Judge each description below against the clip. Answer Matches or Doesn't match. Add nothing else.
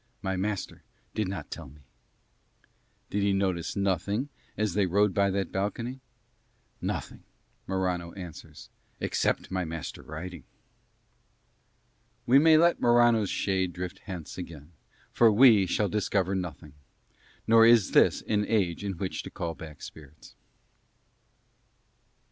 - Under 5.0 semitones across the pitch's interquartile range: Matches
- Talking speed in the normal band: Doesn't match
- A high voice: Doesn't match